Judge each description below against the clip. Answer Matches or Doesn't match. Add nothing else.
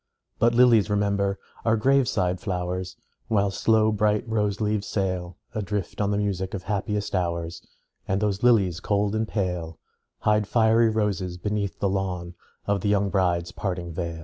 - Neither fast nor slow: Matches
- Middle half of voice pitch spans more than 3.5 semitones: Doesn't match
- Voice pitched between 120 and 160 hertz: Doesn't match